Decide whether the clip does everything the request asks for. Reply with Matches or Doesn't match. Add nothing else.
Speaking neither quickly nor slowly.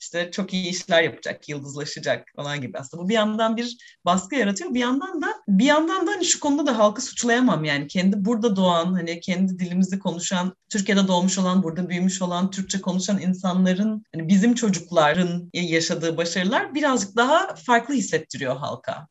Doesn't match